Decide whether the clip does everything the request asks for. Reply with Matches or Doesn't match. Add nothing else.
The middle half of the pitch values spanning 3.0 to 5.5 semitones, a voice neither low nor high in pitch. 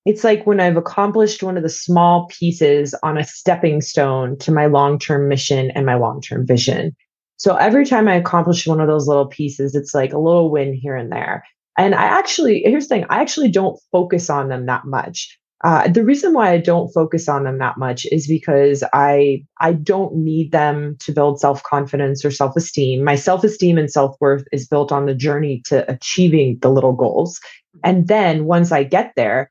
Matches